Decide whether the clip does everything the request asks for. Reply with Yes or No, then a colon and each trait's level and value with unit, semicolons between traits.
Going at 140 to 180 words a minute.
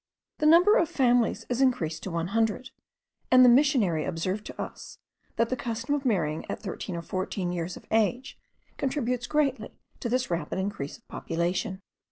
Yes: average, 175 wpm